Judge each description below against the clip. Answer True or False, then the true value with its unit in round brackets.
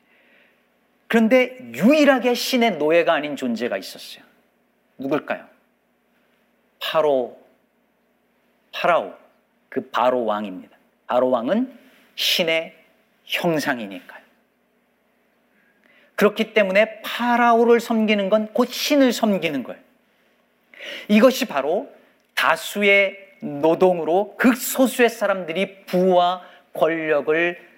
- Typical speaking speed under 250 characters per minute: True (210 characters per minute)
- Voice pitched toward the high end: True (215 Hz)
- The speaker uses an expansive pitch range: True (5.9 semitones)